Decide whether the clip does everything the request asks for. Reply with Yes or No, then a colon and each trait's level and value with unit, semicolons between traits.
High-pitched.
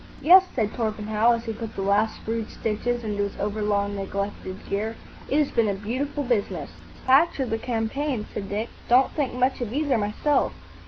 Yes: high, 225 Hz